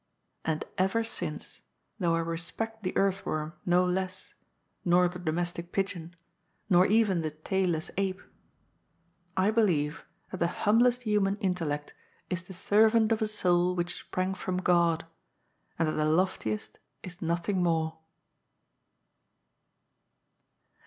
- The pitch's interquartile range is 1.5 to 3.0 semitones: Yes, average, 2.7 semitones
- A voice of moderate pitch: Yes, medium, 180 Hz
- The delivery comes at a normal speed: No, slow, 125 wpm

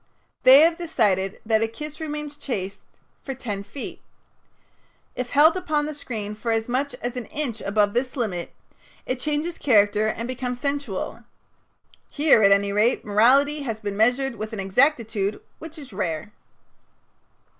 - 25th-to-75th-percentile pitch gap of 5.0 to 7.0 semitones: Yes, wide, 5.4 semitones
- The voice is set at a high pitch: Yes, high, 240 Hz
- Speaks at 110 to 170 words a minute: Yes, average, 155 wpm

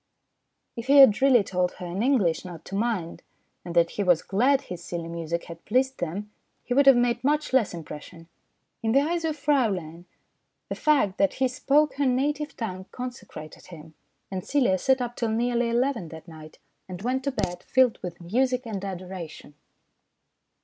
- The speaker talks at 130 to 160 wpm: No, average, 180 wpm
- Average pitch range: No, wide, 6.9 semitones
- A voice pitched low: No, high, 220 Hz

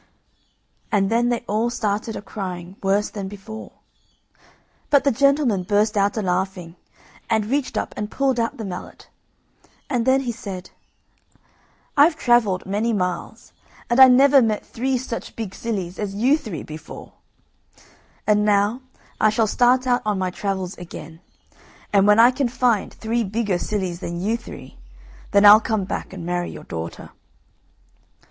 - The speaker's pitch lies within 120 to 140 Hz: No, high, 210 Hz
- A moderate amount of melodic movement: Yes, average, 3.8 semitones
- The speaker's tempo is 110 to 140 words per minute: No, average, 155 wpm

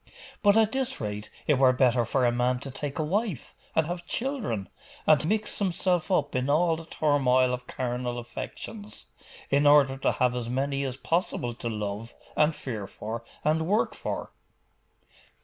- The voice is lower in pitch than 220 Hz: Yes, medium, 140 Hz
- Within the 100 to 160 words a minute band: No, average, 170 wpm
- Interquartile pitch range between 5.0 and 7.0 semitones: Yes, wide, 5.4 semitones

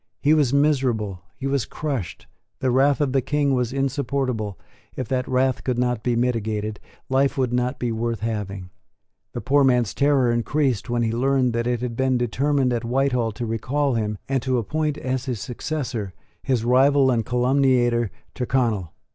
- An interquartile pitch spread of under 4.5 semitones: Yes, average, 2.7 semitones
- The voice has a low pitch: Yes, low, 125 Hz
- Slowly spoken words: No, average, 170 wpm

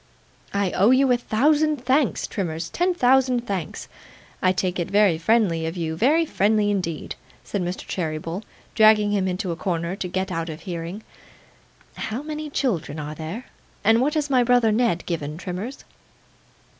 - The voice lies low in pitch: No, high, 200 Hz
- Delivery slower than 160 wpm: No, average, 165 wpm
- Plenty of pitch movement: Yes, wide, 6.5 semitones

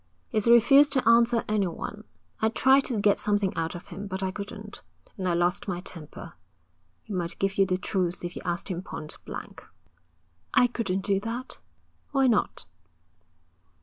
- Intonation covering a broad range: No, average, 4.1 semitones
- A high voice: Yes, high, 200 Hz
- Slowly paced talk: No, average, 165 wpm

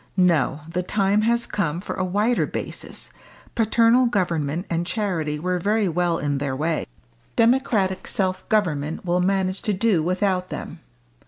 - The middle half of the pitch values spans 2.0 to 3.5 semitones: No, average, 3.9 semitones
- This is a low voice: No, medium, 185 Hz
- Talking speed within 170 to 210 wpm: No, average, 150 wpm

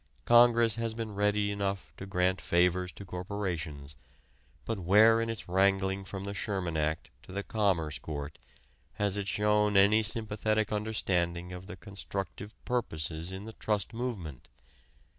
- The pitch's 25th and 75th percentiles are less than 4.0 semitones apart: Yes, average, 2.9 semitones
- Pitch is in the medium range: No, low, 100 Hz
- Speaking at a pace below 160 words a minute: Yes, average, 145 wpm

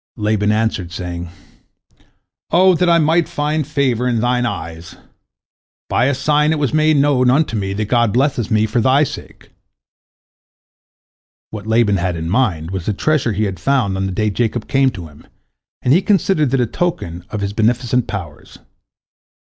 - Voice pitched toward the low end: Yes, low, 120 Hz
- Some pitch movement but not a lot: No, wide, 5.9 semitones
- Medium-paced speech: Yes, average, 175 wpm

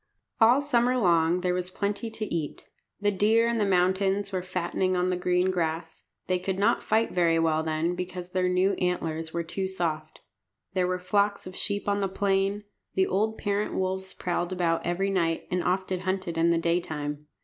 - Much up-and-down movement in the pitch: No, narrow, 2.5 semitones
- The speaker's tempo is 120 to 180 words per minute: No, average, 190 wpm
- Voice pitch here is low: No, medium, 185 Hz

